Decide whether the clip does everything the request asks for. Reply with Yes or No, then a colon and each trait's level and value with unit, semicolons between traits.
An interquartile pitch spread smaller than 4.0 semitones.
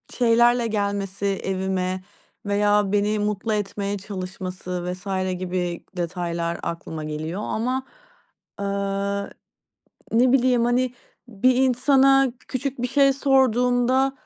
No: average, 4.8 semitones